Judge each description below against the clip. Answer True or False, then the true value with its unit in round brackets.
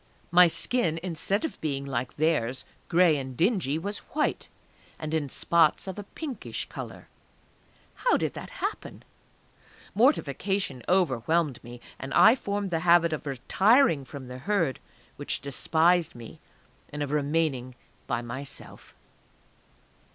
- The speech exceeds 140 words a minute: False (135 wpm)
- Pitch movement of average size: False (5.8 semitones)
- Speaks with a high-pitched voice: False (160 Hz)